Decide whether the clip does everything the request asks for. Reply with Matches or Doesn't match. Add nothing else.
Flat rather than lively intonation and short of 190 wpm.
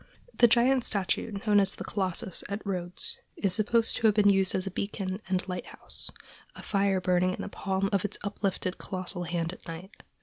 Doesn't match